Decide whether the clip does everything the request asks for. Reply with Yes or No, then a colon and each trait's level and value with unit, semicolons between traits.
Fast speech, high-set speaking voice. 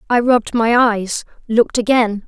No: average, 160 wpm; high, 230 Hz